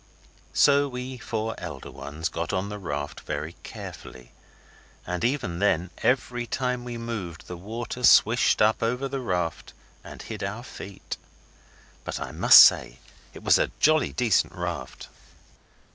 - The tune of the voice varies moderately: No, wide, 6.3 semitones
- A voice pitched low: Yes, low, 105 Hz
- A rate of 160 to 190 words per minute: No, average, 145 wpm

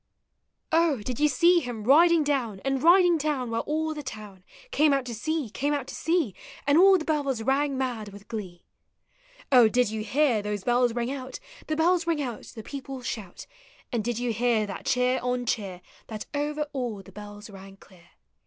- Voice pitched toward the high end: Yes, very high, 250 Hz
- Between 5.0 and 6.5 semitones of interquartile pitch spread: Yes, average, 5.3 semitones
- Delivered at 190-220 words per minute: Yes, average, 195 wpm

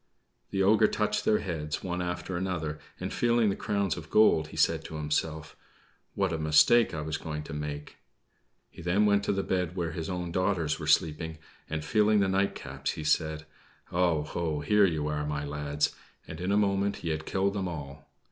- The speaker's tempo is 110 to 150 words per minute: No, average, 195 wpm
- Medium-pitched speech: No, very low, 85 Hz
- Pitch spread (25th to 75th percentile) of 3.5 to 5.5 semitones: Yes, average, 4.2 semitones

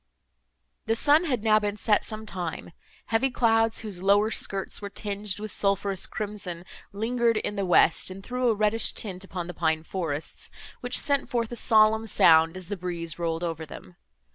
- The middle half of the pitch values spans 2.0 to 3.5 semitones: No, average, 4.0 semitones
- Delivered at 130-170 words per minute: No, average, 180 wpm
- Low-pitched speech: No, high, 205 Hz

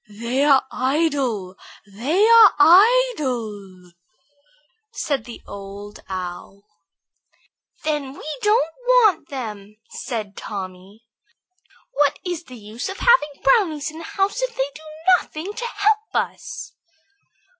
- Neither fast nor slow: No, slow, 115 wpm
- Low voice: No, very high, 285 Hz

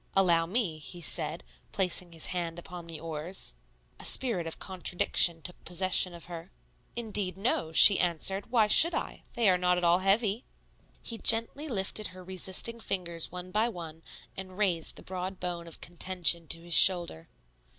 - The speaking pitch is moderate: Yes, medium, 180 Hz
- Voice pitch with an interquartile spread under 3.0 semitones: Yes, narrow, 2.4 semitones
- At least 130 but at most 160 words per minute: No, average, 170 wpm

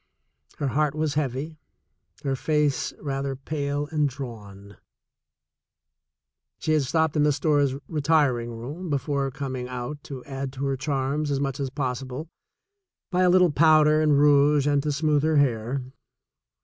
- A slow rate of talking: No, average, 150 wpm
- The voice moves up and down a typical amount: No, narrow, 2.2 semitones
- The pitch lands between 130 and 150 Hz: Yes, medium, 140 Hz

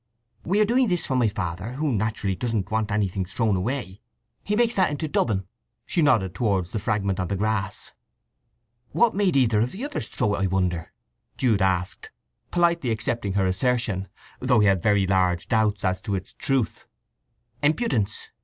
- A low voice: Yes, low, 110 Hz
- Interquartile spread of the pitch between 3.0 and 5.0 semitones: No, wide, 5.6 semitones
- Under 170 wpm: No, average, 175 wpm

